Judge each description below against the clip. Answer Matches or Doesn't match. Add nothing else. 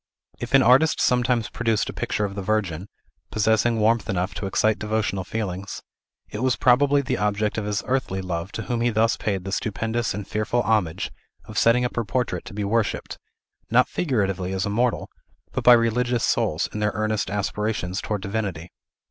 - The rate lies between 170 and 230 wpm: Matches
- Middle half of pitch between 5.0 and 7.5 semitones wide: Doesn't match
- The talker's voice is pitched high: Doesn't match